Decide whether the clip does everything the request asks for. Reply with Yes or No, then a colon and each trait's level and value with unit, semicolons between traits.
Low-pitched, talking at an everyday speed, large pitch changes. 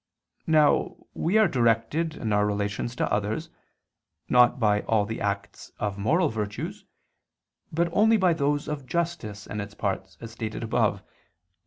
Yes: low, 115 Hz; average, 155 wpm; wide, 7.2 semitones